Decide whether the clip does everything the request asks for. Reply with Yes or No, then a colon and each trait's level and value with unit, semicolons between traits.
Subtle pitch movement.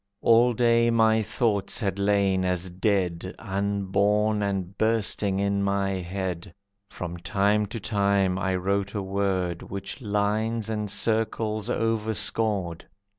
Yes: narrow, 2.3 semitones